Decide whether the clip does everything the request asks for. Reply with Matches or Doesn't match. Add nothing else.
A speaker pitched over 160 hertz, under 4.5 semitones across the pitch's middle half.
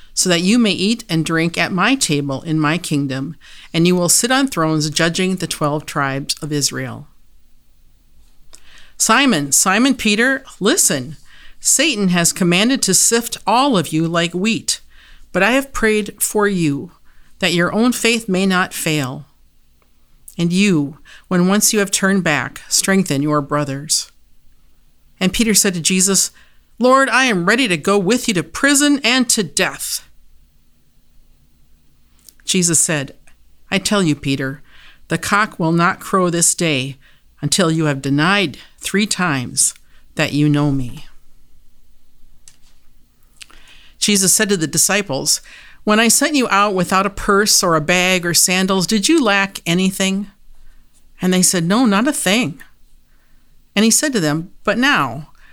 Doesn't match